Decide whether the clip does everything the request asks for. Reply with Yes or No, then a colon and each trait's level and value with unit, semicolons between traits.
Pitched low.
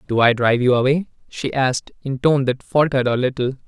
Yes: low, 130 Hz